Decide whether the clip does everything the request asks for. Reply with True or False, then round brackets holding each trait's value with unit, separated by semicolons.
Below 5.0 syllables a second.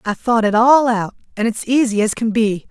False (5.5 syllables/s)